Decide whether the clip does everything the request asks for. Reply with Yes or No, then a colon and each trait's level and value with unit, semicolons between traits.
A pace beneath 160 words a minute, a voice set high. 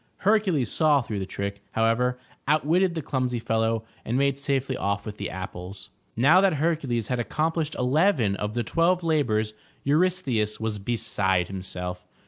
No: average, 150 wpm; low, 125 Hz